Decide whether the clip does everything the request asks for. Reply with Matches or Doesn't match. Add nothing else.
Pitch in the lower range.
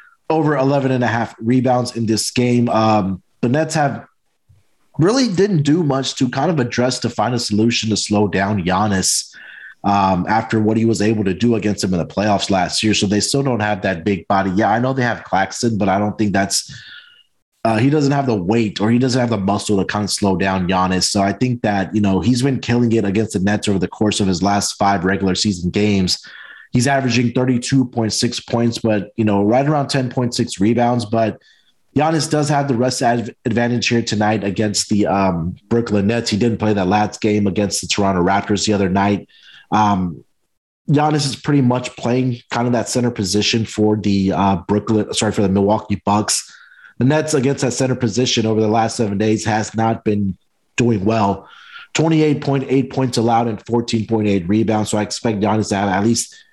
Matches